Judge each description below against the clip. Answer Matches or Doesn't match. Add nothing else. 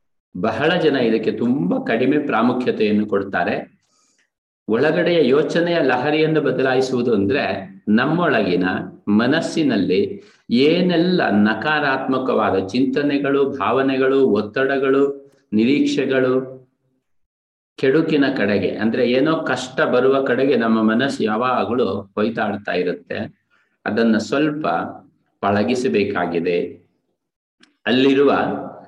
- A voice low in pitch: Matches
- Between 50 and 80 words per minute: Matches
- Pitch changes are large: Doesn't match